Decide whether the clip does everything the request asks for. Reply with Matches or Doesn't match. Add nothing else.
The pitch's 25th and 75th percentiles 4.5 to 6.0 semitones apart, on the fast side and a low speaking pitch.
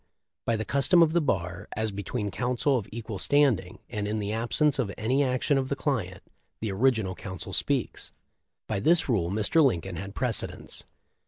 Doesn't match